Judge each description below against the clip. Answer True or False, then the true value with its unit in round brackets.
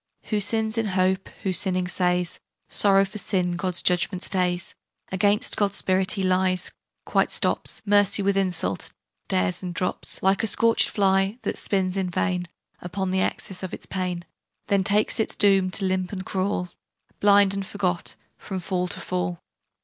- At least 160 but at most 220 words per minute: True (165 wpm)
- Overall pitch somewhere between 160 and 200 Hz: True (190 Hz)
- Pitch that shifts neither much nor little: False (1.7 semitones)